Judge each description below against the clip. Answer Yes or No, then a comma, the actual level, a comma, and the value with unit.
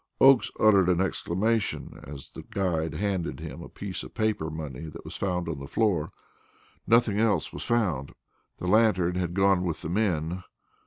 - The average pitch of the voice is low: Yes, very low, 90 Hz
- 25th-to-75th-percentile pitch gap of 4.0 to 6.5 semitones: Yes, average, 4.3 semitones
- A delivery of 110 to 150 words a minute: No, average, 165 wpm